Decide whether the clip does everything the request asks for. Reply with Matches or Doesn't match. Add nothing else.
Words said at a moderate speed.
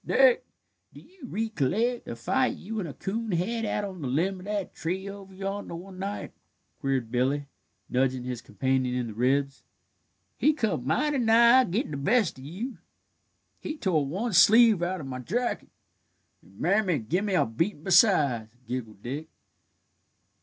Matches